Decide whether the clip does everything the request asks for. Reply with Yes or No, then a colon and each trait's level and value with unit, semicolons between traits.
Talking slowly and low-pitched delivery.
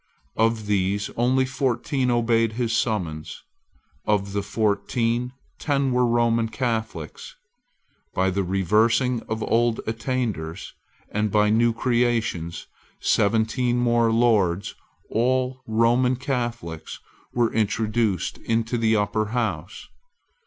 Yes: slow, 105 wpm; low, 115 Hz